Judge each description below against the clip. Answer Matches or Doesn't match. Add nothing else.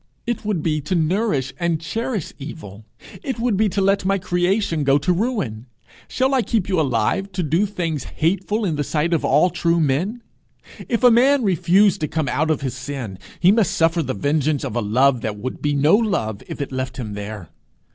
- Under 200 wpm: Doesn't match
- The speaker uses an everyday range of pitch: Doesn't match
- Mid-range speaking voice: Matches